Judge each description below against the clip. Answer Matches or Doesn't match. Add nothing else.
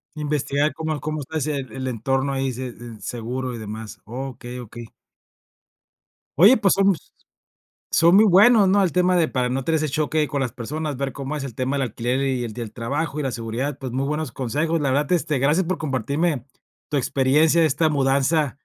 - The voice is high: Doesn't match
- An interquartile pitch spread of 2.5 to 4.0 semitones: Matches